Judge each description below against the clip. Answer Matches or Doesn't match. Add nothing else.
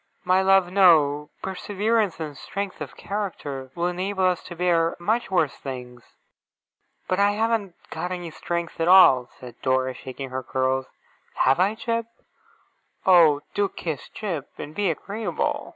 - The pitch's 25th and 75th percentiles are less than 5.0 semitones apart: Doesn't match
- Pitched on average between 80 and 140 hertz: Doesn't match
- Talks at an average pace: Matches